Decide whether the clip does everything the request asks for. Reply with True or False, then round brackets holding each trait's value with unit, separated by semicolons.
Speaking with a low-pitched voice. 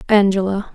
False (200 Hz)